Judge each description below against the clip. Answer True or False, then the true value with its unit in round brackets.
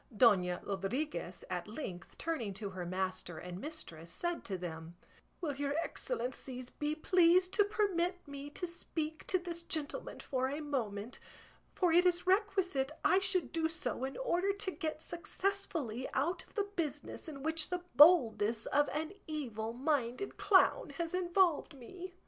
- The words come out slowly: False (155 wpm)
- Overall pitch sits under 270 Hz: False (305 Hz)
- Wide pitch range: True (7.2 semitones)